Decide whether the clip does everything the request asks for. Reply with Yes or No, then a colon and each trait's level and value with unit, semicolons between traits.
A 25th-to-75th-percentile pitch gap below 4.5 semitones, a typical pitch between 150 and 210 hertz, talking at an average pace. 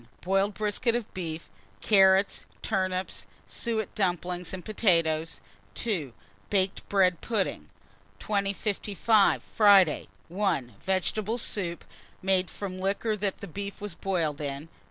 No: average, 2.7 semitones; high, 190 Hz; slow, 110 wpm